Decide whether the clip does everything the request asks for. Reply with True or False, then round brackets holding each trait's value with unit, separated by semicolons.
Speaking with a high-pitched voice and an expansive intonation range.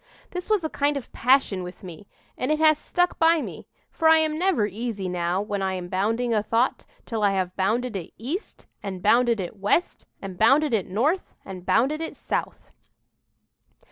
True (225 Hz; 7.9 semitones)